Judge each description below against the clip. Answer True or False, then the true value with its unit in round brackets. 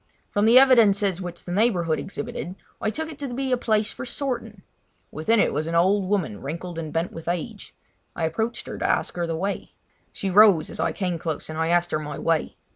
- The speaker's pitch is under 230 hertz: True (185 Hz)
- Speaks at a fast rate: True (215 wpm)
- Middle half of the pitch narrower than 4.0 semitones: False (5.0 semitones)